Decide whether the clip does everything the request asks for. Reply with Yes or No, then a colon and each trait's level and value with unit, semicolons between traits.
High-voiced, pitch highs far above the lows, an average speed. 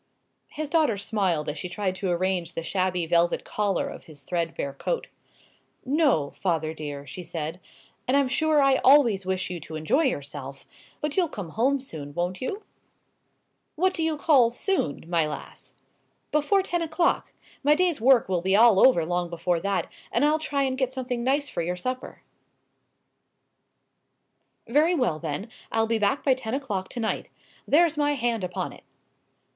Yes: high, 215 Hz; wide, 8.5 semitones; average, 170 wpm